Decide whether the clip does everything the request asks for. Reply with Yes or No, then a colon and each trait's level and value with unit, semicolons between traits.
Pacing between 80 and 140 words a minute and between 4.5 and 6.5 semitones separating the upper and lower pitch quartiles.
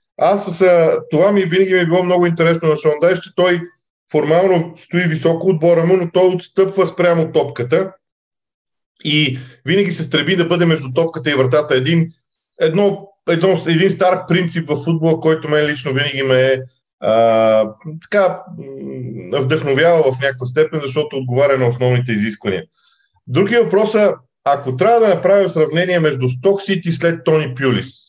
No: average, 155 wpm; average, 4.8 semitones